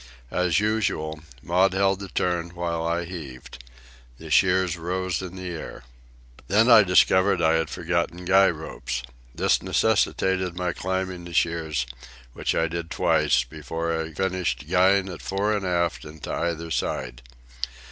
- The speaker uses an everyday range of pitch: No, narrow, 2.3 semitones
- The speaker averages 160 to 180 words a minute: No, average, 150 wpm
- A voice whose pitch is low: Yes, very low, 85 Hz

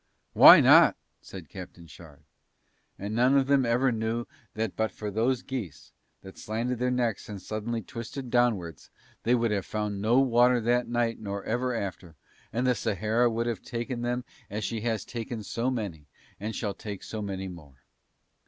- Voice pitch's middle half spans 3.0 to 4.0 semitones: Yes, average, 3.3 semitones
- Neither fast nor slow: Yes, average, 175 wpm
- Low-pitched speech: Yes, low, 115 Hz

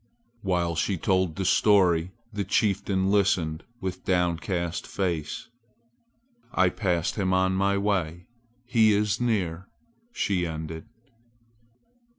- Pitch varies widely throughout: No, narrow, 2.6 semitones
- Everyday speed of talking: No, slow, 110 wpm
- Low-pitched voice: Yes, very low, 95 Hz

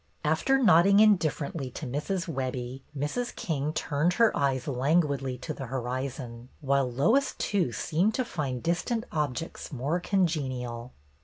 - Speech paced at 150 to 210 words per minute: No, average, 140 wpm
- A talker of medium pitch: Yes, medium, 145 Hz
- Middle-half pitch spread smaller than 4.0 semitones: No, average, 5.2 semitones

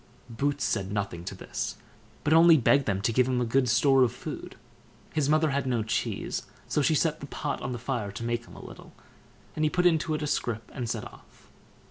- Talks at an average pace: No, fast, 225 wpm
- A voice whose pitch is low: Yes, low, 130 Hz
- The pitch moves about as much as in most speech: Yes, average, 4.5 semitones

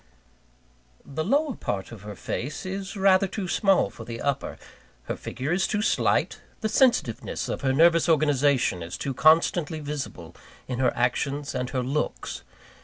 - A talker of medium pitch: Yes, medium, 145 Hz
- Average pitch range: No, wide, 6.7 semitones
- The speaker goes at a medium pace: Yes, average, 160 wpm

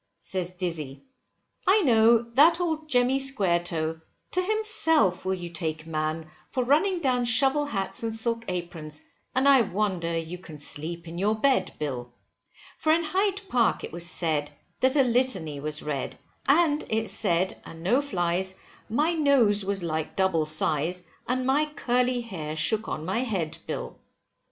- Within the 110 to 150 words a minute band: No, average, 160 wpm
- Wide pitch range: Yes, wide, 8.0 semitones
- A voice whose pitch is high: Yes, high, 200 Hz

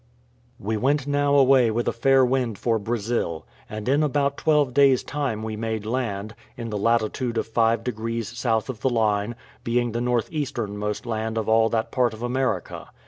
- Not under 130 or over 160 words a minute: No, average, 185 wpm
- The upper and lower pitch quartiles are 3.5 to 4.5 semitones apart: No, average, 2.9 semitones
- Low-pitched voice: Yes, low, 115 Hz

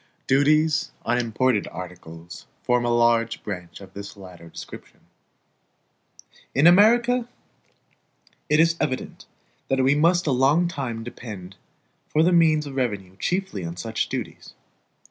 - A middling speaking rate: No, slow, 130 wpm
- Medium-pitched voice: No, low, 125 Hz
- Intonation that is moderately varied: No, wide, 7.5 semitones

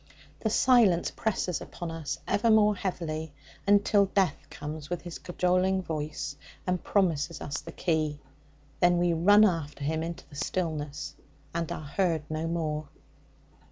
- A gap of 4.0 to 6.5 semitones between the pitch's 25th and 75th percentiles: No, average, 3.4 semitones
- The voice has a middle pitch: Yes, medium, 170 Hz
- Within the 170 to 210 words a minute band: No, average, 145 wpm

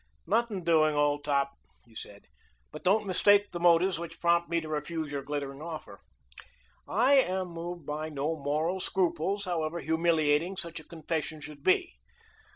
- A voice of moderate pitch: Yes, medium, 165 Hz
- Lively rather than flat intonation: No, average, 3.1 semitones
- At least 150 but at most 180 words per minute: Yes, average, 160 wpm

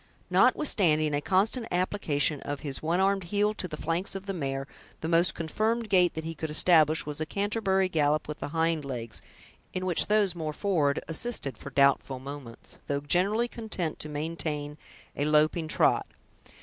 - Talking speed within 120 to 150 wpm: No, average, 175 wpm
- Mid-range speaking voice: Yes, medium, 160 Hz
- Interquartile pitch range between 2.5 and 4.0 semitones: No, average, 4.6 semitones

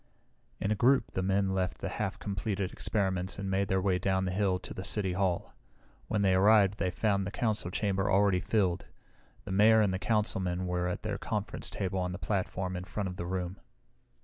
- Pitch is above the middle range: No, very low, 95 Hz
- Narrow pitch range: Yes, narrow, 1.6 semitones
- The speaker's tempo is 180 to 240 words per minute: Yes, fast, 205 wpm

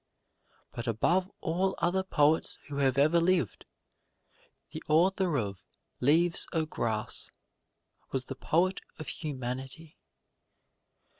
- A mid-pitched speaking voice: Yes, medium, 155 Hz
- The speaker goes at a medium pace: No, slow, 105 wpm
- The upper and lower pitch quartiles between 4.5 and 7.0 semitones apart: Yes, average, 4.8 semitones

